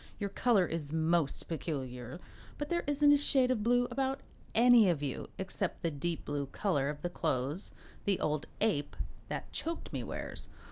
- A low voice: No, medium, 175 Hz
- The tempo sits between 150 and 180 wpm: Yes, average, 175 wpm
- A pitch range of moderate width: No, wide, 8.9 semitones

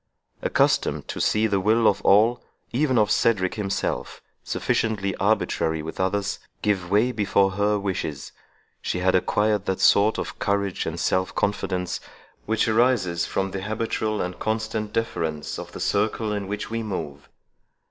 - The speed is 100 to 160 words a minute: Yes, average, 150 wpm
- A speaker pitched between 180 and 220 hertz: No, low, 100 Hz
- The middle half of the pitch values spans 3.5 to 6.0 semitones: No, average, 2.7 semitones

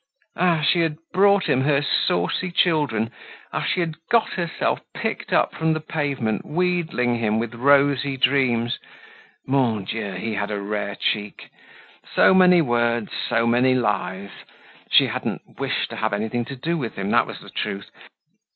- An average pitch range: No, wide, 6.3 semitones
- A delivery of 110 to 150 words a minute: No, average, 160 wpm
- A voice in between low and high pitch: No, low, 125 Hz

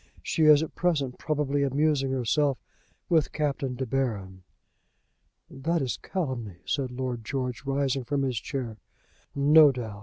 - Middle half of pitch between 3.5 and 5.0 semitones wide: No, average, 2.9 semitones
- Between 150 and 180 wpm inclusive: No, average, 140 wpm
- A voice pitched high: No, low, 135 Hz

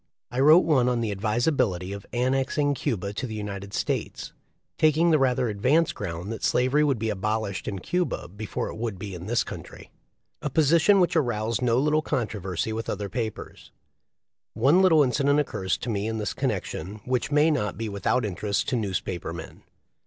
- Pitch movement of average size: No, wide, 5.7 semitones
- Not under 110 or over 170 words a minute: No, average, 180 wpm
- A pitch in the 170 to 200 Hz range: No, low, 115 Hz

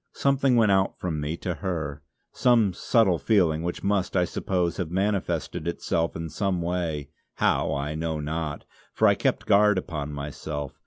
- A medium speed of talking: Yes, average, 165 wpm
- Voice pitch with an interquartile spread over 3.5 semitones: Yes, average, 4.0 semitones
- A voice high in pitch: No, very low, 85 Hz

